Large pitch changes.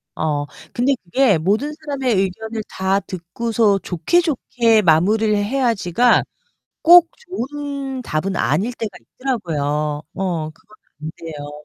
Yes: wide, 7.4 semitones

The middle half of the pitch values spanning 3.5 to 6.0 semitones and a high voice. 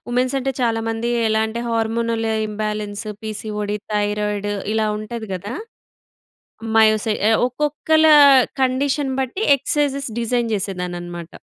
No: average, 3.1 semitones; high, 225 Hz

